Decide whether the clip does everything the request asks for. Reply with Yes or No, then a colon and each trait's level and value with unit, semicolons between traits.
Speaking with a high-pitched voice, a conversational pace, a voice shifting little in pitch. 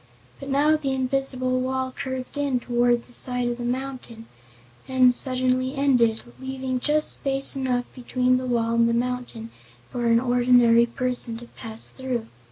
Yes: very high, 255 Hz; average, 160 wpm; narrow, 1.6 semitones